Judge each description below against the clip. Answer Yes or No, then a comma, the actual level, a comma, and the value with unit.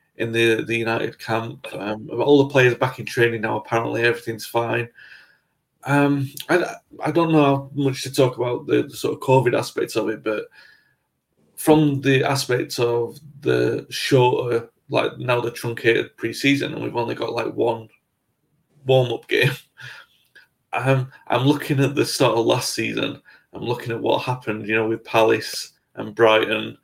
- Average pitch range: Yes, average, 3.4 semitones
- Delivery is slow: No, average, 170 wpm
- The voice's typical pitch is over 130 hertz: No, low, 125 Hz